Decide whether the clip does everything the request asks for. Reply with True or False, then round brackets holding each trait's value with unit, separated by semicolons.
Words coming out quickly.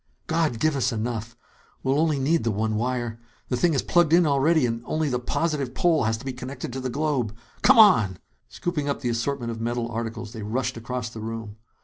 True (215 wpm)